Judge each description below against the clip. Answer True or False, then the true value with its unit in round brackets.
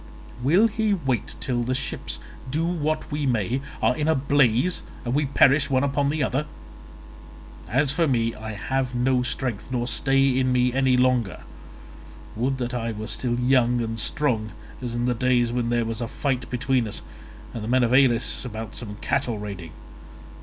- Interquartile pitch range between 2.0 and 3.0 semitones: True (2.6 semitones)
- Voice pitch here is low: True (125 Hz)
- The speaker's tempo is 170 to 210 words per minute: True (180 wpm)